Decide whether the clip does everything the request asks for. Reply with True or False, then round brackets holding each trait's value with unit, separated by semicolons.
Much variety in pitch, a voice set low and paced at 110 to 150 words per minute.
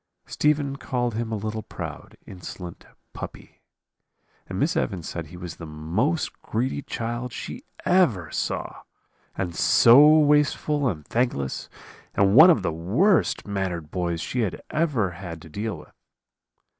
True (8.2 semitones; 110 Hz; 140 wpm)